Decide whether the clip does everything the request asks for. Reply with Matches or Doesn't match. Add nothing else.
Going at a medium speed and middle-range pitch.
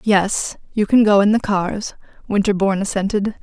Doesn't match